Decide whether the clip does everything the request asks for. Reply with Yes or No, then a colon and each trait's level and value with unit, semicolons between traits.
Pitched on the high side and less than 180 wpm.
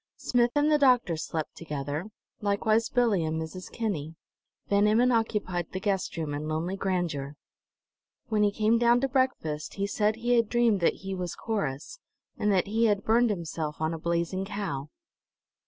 Yes: high, 200 Hz; average, 170 wpm